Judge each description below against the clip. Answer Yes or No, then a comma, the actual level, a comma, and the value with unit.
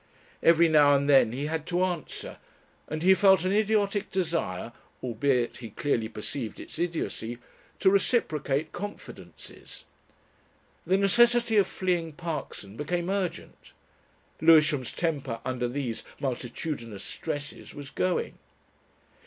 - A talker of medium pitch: Yes, medium, 155 Hz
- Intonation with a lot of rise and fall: Yes, wide, 5.7 semitones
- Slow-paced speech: Yes, slow, 120 wpm